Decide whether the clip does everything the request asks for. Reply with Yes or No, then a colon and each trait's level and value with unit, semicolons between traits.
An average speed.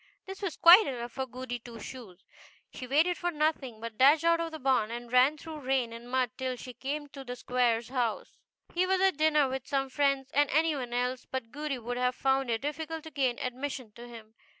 No: fast, 220 wpm